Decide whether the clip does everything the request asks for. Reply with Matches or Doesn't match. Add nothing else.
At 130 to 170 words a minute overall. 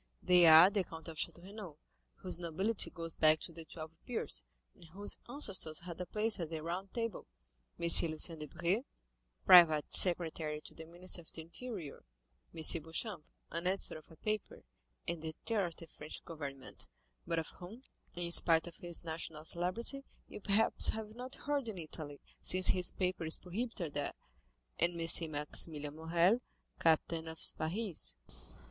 Matches